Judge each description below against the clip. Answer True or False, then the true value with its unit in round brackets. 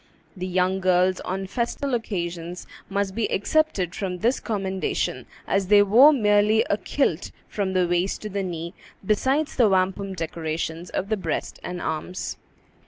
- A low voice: False (190 Hz)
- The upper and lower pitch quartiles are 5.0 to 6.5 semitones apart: False (2.8 semitones)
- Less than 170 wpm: True (155 wpm)